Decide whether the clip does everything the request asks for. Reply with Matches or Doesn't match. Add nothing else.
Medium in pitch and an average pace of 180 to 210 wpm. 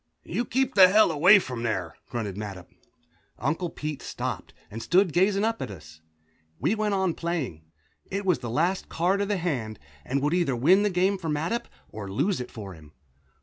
Matches